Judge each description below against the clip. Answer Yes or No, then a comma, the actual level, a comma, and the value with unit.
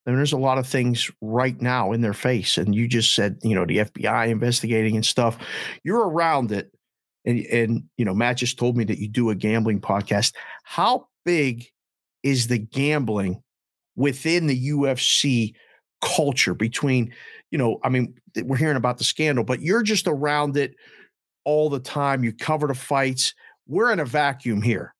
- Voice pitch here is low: Yes, low, 125 Hz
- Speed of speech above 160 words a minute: Yes, average, 185 wpm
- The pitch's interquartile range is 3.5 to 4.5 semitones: Yes, average, 4.0 semitones